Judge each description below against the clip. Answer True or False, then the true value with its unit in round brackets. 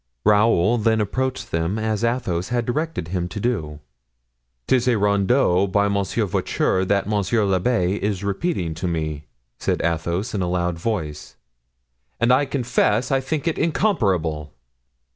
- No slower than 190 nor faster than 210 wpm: False (145 wpm)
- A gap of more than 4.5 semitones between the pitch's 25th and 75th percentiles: True (5.3 semitones)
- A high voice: False (100 Hz)